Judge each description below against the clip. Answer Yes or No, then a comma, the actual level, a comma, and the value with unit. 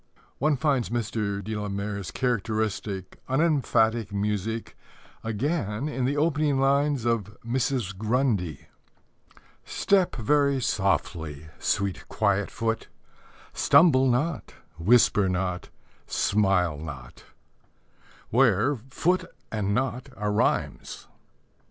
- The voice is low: Yes, low, 110 Hz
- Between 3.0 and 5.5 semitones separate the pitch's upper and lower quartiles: Yes, average, 5.2 semitones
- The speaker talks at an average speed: No, slow, 95 wpm